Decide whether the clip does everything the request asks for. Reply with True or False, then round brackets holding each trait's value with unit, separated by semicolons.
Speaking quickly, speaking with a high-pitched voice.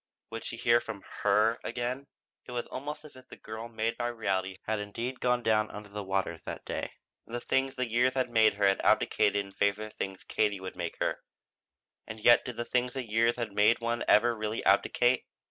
False (220 wpm; 115 Hz)